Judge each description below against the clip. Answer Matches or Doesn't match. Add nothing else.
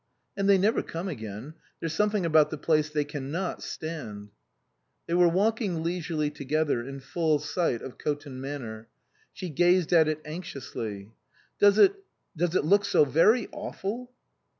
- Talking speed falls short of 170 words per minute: Doesn't match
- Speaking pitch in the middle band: Matches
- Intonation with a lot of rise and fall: Doesn't match